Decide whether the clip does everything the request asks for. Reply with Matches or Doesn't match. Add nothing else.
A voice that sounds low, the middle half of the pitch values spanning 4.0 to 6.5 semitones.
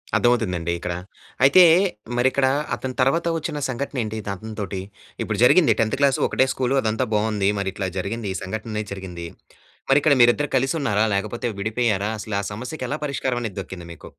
Matches